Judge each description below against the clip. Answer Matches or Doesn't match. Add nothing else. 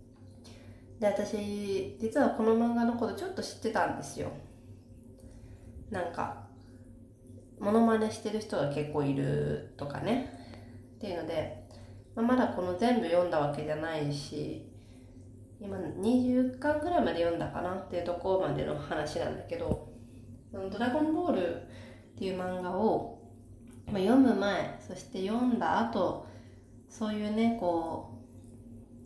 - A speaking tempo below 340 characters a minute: Matches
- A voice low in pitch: Doesn't match